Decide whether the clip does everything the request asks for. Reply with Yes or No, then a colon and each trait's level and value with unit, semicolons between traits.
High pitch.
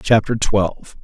No: low, 105 Hz